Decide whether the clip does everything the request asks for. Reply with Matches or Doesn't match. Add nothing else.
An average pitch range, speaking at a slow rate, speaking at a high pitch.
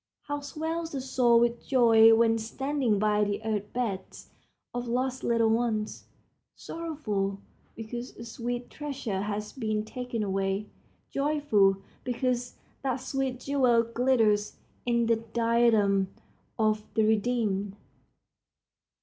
Matches